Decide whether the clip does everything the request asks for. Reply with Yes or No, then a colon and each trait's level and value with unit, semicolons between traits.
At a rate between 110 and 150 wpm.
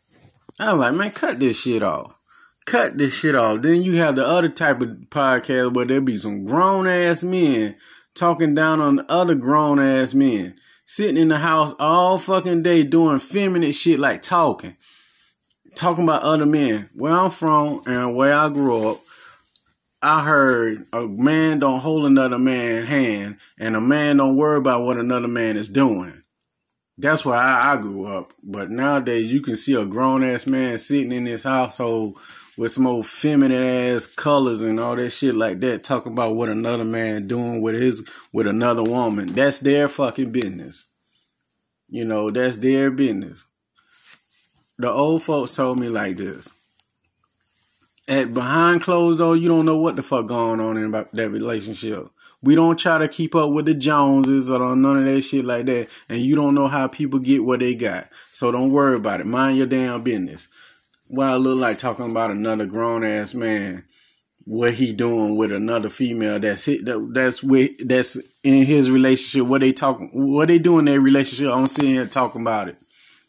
No: average, 185 wpm